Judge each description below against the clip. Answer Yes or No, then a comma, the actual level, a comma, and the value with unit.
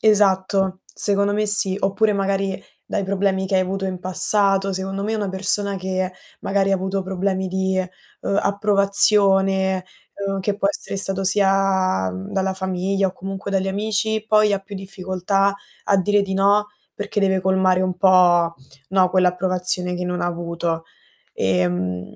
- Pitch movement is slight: Yes, narrow, 1.2 semitones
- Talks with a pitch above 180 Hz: Yes, high, 190 Hz